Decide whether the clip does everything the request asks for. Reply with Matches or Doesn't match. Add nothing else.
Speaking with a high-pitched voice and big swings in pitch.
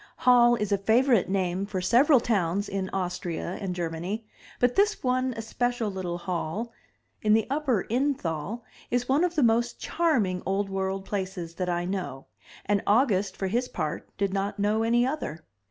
Doesn't match